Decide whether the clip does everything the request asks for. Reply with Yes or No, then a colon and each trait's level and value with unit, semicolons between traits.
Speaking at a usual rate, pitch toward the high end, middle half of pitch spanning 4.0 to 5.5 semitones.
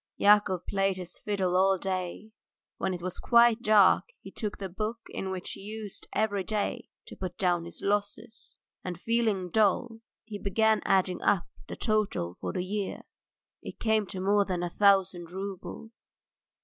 No: average, 165 wpm; high, 195 Hz; average, 2.7 semitones